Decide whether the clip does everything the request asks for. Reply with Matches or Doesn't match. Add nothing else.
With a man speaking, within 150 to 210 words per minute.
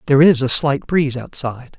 Matches